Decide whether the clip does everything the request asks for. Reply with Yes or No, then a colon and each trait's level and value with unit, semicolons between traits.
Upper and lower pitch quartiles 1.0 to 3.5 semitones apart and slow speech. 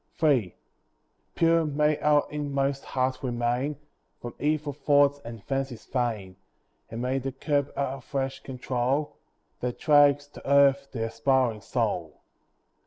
Yes: narrow, 2.6 semitones; slow, 125 wpm